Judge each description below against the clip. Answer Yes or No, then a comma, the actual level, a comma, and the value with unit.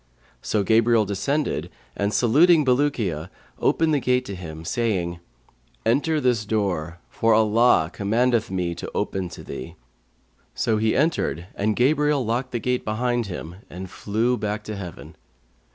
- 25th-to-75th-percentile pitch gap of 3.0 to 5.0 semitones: Yes, average, 4.5 semitones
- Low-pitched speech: Yes, low, 110 Hz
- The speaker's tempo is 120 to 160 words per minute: Yes, average, 145 wpm